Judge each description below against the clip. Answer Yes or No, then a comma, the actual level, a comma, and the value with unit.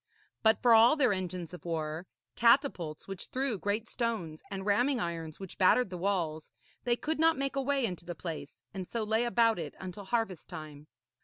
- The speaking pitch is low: No, high, 200 Hz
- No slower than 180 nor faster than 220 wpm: Yes, average, 190 wpm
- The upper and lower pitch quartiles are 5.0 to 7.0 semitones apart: Yes, wide, 5.6 semitones